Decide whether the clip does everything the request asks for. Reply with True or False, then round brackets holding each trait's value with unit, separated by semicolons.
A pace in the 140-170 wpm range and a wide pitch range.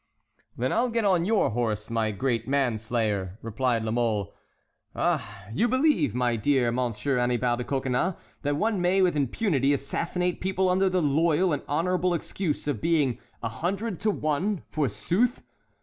True (160 wpm; 7.4 semitones)